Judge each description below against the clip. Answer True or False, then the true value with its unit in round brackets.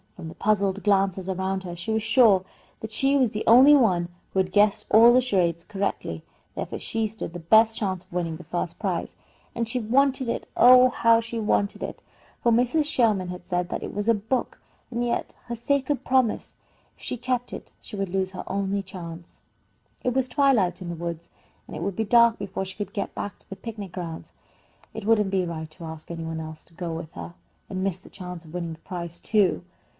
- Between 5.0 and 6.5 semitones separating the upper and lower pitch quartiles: False (4.6 semitones)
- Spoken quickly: True (220 wpm)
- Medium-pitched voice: False (200 Hz)